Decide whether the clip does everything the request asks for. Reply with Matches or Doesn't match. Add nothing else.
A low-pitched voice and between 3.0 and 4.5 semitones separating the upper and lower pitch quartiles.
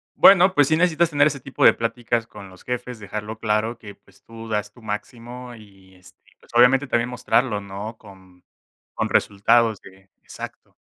Matches